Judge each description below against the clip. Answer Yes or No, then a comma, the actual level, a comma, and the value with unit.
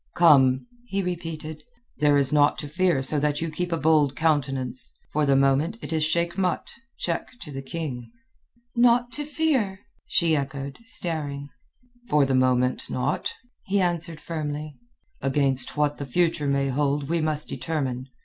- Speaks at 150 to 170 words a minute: Yes, average, 155 wpm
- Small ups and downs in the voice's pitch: No, average, 3.6 semitones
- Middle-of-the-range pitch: Yes, medium, 150 Hz